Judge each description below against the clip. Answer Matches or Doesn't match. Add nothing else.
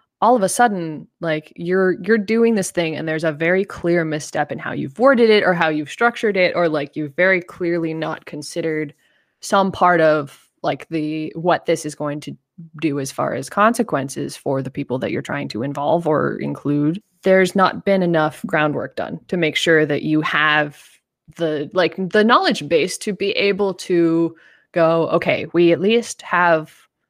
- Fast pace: Doesn't match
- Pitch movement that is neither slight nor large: Matches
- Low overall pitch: Doesn't match